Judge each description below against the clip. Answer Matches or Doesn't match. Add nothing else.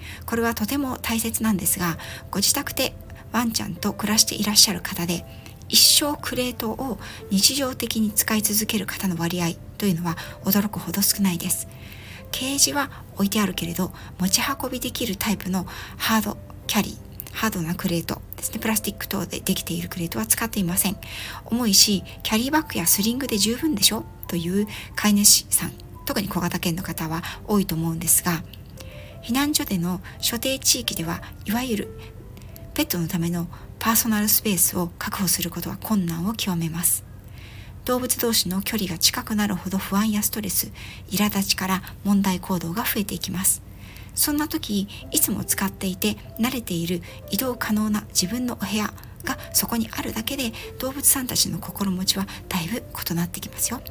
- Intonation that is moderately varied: Matches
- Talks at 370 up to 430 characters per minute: Doesn't match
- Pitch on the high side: Matches